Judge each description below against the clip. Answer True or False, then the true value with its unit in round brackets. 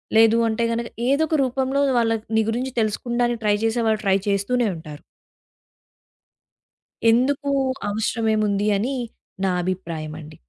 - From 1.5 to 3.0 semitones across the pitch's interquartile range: False (3.5 semitones)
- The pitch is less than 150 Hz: False (225 Hz)